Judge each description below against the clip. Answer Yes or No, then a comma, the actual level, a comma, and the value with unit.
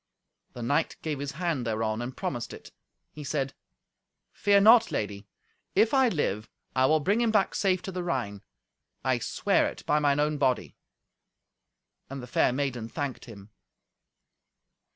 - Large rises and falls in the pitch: Yes, wide, 6.5 semitones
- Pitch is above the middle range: No, medium, 140 Hz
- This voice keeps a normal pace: Yes, average, 155 wpm